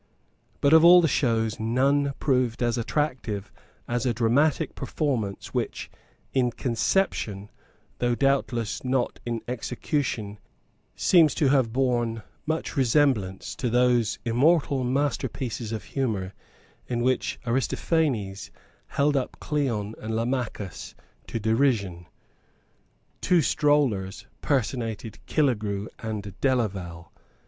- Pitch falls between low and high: No, low, 120 Hz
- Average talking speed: No, slow, 105 wpm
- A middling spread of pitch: Yes, average, 4.0 semitones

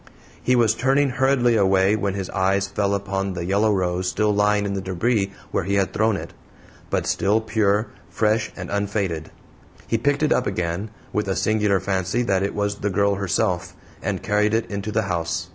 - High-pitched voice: No, low, 100 Hz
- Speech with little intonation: Yes, narrow, 2.2 semitones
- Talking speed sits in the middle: Yes, average, 195 wpm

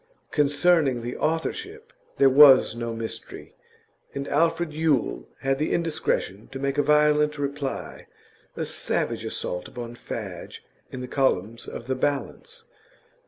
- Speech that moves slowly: Yes, slow, 130 wpm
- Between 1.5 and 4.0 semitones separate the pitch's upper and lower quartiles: Yes, average, 3.4 semitones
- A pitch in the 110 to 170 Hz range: Yes, medium, 140 Hz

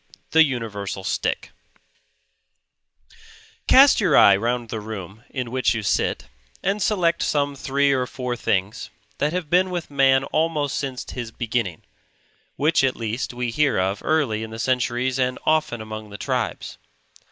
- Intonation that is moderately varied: Yes, average, 4.9 semitones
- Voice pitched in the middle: No, low, 125 Hz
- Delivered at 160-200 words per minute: No, average, 150 wpm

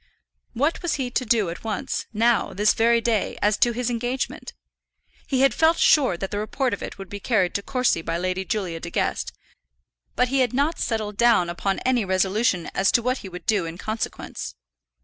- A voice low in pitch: No, high, 220 Hz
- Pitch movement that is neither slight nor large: Yes, average, 4.5 semitones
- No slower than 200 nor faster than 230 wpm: Yes, fast, 205 wpm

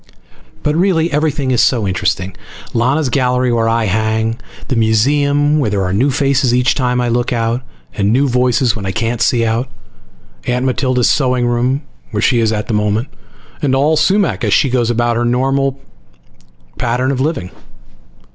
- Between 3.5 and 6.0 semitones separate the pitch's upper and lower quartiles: No, average, 3.1 semitones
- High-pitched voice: No, low, 125 Hz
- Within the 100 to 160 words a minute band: No, average, 175 wpm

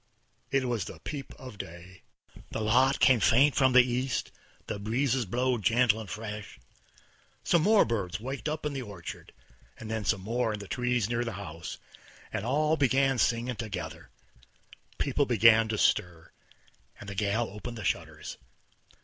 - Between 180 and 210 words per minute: No, average, 160 wpm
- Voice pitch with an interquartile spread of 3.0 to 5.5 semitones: Yes, average, 3.8 semitones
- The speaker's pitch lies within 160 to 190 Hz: No, low, 115 Hz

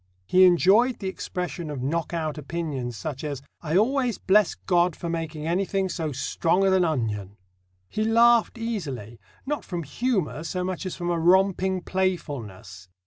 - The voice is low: No, medium, 175 Hz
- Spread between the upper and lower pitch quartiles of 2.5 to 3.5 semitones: No, average, 4.2 semitones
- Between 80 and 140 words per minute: No, average, 160 wpm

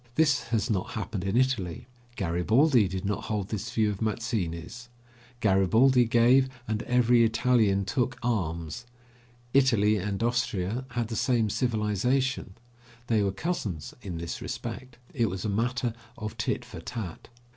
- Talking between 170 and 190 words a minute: No, average, 145 wpm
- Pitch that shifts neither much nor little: Yes, average, 3.9 semitones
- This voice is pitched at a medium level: No, low, 110 Hz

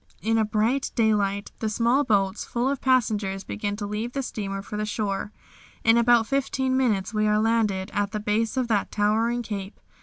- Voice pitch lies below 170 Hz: No, high, 215 Hz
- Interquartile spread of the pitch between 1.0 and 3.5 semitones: Yes, narrow, 2.4 semitones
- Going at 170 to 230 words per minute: Yes, average, 190 wpm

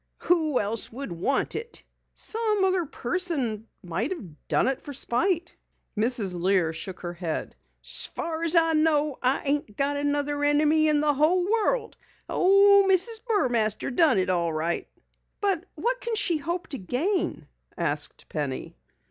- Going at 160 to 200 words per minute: No, average, 150 wpm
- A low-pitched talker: No, very high, 290 Hz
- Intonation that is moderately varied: No, wide, 8.8 semitones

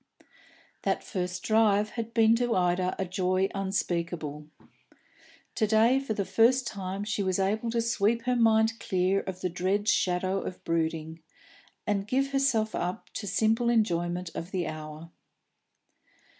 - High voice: Yes, high, 195 Hz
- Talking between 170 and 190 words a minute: No, average, 145 wpm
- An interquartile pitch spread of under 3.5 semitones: No, average, 3.8 semitones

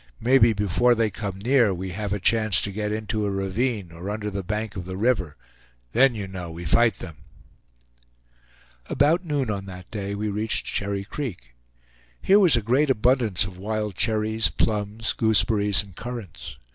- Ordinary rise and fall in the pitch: Yes, average, 3.0 semitones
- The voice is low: Yes, low, 105 Hz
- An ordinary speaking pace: Yes, average, 170 wpm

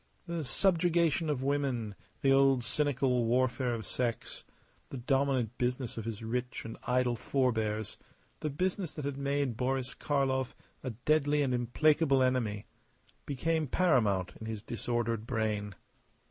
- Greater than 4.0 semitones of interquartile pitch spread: No, average, 3.5 semitones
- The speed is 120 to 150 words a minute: Yes, slow, 135 wpm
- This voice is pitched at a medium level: No, low, 130 Hz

